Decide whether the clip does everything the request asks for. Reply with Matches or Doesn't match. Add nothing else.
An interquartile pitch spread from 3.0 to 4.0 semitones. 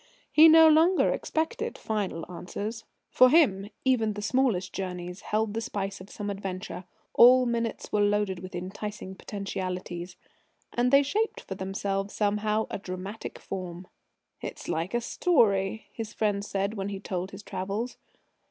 Matches